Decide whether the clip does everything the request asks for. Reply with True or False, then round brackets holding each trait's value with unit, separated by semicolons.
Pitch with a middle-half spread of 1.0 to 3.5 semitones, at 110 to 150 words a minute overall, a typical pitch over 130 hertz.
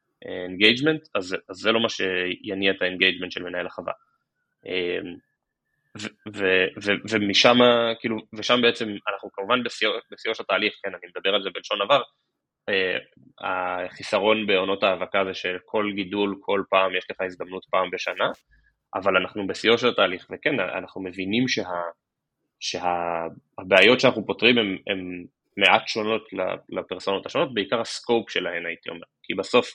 False (3.2 semitones; 140 wpm; 100 Hz)